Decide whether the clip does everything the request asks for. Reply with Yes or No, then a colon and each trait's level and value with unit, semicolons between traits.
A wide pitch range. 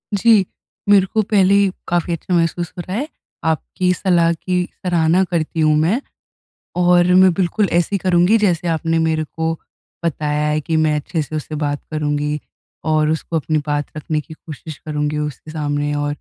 No: average, 3.0 semitones